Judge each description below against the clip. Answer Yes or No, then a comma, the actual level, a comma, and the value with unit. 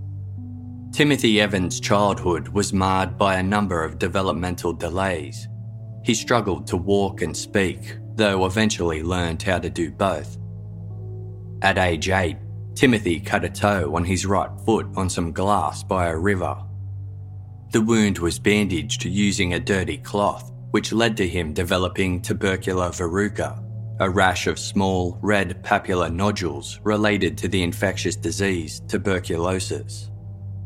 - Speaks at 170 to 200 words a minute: No, slow, 135 wpm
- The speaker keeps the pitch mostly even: Yes, narrow, 2.1 semitones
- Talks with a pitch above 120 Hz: No, low, 100 Hz